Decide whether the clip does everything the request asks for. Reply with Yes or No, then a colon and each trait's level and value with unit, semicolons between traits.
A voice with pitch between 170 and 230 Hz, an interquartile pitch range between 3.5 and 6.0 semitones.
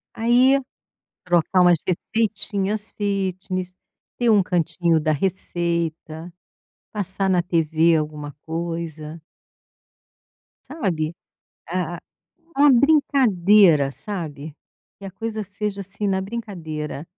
Yes: medium, 185 Hz; average, 4.0 semitones